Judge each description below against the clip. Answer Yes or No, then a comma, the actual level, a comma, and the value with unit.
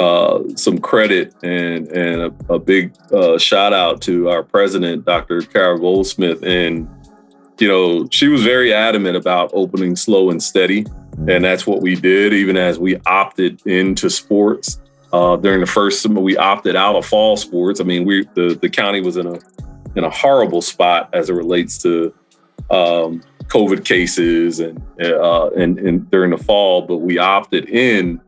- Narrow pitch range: Yes, narrow, 2.1 semitones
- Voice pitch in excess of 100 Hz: No, very low, 90 Hz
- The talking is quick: No, average, 175 wpm